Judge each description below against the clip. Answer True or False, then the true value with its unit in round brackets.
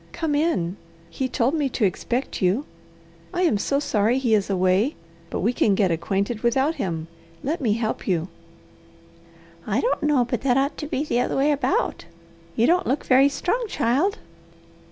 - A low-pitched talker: False (250 Hz)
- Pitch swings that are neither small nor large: False (6.0 semitones)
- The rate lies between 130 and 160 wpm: False (175 wpm)